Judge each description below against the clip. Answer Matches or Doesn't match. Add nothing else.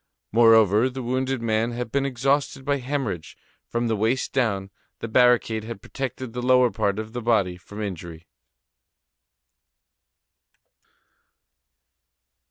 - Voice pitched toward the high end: Doesn't match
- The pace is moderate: Doesn't match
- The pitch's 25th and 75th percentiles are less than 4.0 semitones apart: Matches